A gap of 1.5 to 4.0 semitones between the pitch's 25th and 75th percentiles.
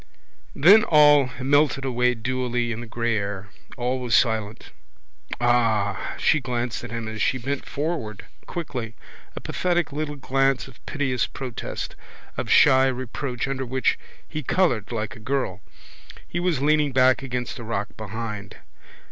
Yes: average, 3.3 semitones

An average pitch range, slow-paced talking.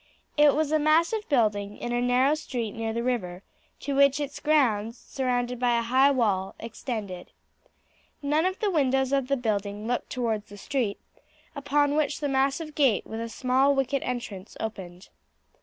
No: average, 4.3 semitones; average, 170 wpm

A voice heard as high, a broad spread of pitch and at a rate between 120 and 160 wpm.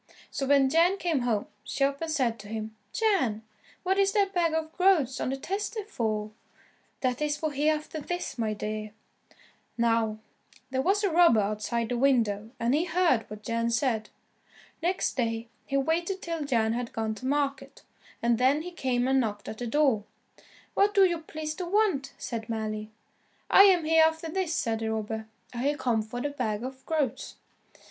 No: very high, 270 Hz; wide, 6.3 semitones; average, 180 wpm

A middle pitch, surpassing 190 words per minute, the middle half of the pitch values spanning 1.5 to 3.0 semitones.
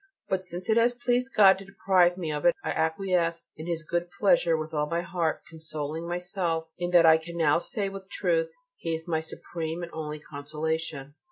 Yes: medium, 170 Hz; average, 200 wpm; average, 2.7 semitones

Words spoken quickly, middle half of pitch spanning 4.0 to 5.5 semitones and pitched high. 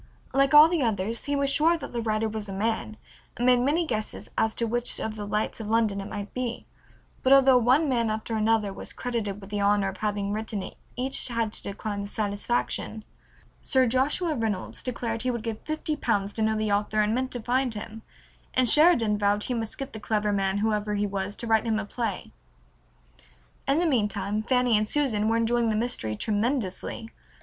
No: fast, 210 wpm; average, 3.1 semitones; high, 225 Hz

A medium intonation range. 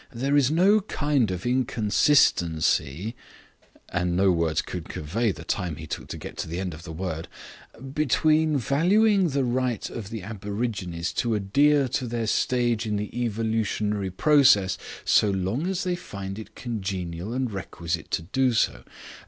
No: wide, 6.2 semitones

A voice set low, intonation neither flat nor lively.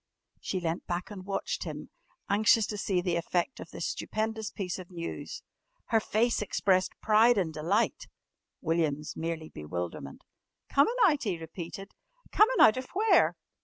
No: high, 190 Hz; average, 4.7 semitones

